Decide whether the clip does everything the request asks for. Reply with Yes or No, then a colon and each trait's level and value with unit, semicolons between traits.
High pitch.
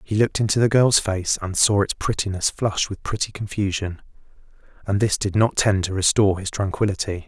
No: low, 100 Hz